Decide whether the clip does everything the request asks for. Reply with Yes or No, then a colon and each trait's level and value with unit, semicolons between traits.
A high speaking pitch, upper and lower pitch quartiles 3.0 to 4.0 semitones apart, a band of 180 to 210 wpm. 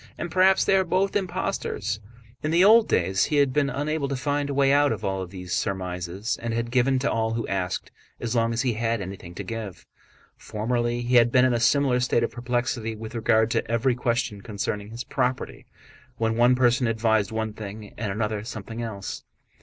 No: low, 115 Hz; average, 3.3 semitones; average, 200 wpm